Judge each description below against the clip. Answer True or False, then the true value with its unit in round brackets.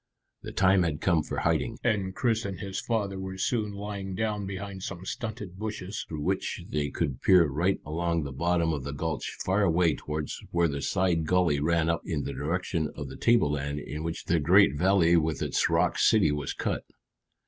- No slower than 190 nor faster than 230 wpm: True (195 wpm)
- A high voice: False (85 Hz)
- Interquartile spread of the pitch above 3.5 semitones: True (4.0 semitones)